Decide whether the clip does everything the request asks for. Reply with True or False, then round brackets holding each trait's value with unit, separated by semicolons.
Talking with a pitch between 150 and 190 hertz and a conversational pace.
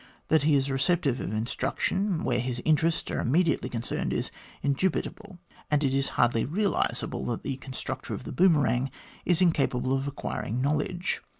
False (140 Hz; 165 wpm)